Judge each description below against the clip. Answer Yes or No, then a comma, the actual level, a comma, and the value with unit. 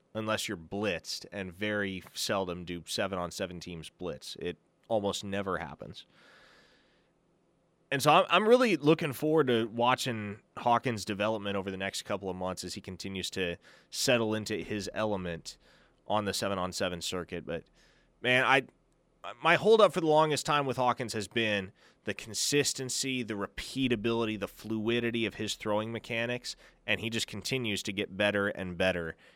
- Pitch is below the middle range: Yes, low, 110 Hz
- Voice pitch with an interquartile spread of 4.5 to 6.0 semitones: Yes, average, 4.8 semitones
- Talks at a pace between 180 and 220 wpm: No, average, 160 wpm